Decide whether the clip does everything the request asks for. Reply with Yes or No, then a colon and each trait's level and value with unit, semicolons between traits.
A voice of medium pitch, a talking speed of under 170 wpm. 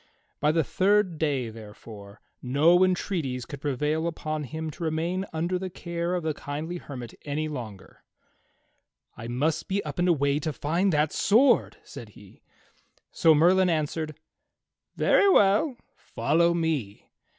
Yes: medium, 155 Hz; average, 140 wpm